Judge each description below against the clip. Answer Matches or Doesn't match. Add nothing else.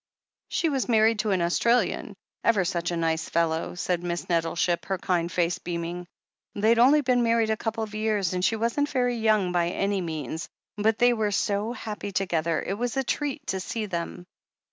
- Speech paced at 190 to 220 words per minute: Matches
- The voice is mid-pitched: Doesn't match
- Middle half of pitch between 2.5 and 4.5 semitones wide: Doesn't match